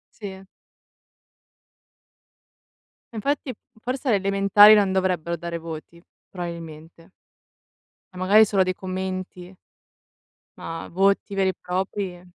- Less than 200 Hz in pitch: Yes, high, 190 Hz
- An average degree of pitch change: No, narrow, 2.3 semitones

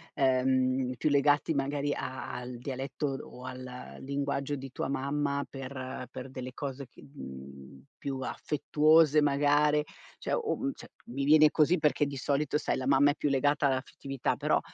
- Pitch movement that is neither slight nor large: No, narrow, 2.0 semitones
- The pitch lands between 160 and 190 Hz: No, medium, 140 Hz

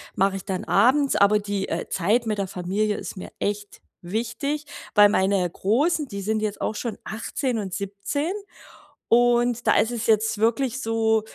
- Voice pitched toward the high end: Yes, high, 215 Hz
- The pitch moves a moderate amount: Yes, average, 3.2 semitones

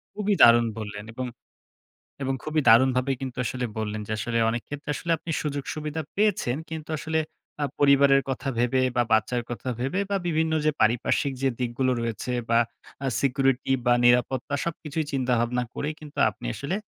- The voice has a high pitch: No, low, 135 Hz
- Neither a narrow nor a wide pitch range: Yes, average, 3.8 semitones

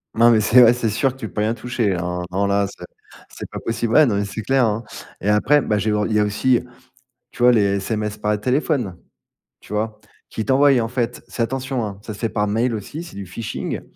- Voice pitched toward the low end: Yes, low, 110 Hz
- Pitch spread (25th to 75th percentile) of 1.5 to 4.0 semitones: Yes, average, 2.9 semitones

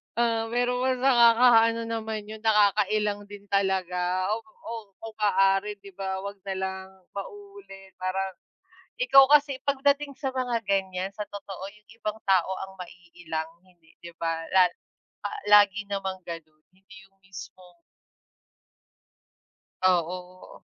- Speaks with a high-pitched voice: Yes, high, 200 Hz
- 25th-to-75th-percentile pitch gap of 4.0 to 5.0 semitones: No, average, 3.4 semitones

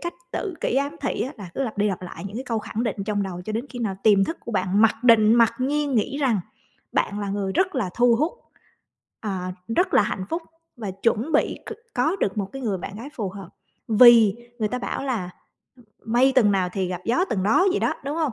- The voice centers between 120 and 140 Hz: No, high, 225 Hz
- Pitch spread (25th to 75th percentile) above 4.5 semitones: Yes, average, 5.1 semitones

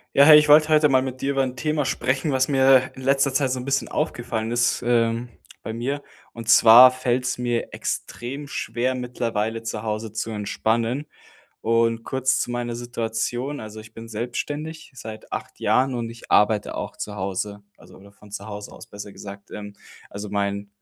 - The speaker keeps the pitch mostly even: No, average, 3.2 semitones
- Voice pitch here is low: Yes, low, 120 Hz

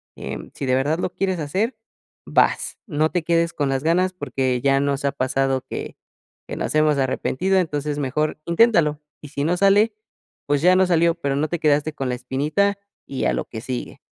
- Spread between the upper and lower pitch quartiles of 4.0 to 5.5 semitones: Yes, average, 4.4 semitones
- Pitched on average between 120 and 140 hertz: No, medium, 150 Hz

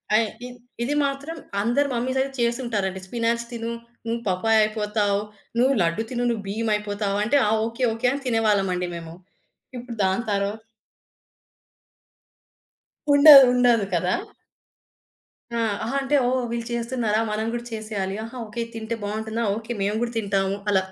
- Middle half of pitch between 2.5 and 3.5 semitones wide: Yes, average, 2.9 semitones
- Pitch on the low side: No, high, 225 Hz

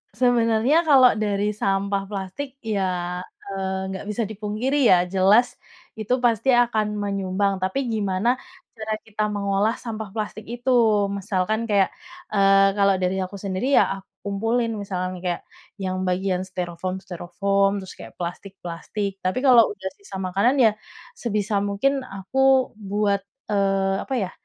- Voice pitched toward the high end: Yes, high, 200 Hz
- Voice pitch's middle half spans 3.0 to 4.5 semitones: No, narrow, 2.6 semitones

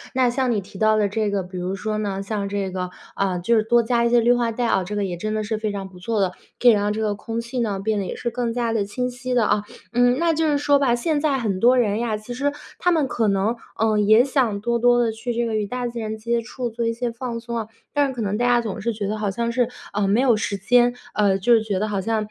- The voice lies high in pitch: Yes, high, 225 Hz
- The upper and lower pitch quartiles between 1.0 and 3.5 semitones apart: Yes, average, 2.9 semitones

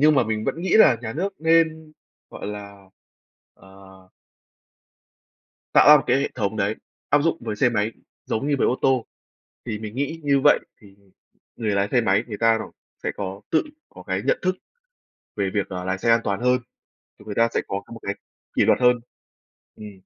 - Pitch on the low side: Yes, low, 115 Hz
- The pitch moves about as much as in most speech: No, wide, 5.7 semitones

